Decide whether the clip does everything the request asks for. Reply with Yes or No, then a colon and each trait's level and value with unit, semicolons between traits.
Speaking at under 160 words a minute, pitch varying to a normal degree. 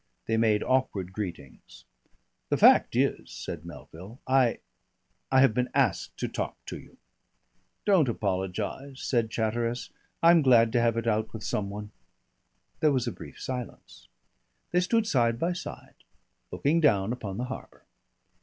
Yes: average, 150 wpm; average, 3.9 semitones